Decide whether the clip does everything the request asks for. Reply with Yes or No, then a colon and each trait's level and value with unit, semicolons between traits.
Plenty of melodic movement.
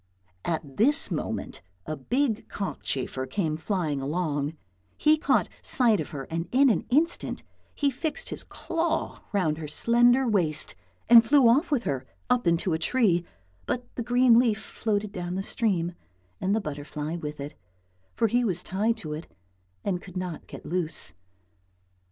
Yes: wide, 7.2 semitones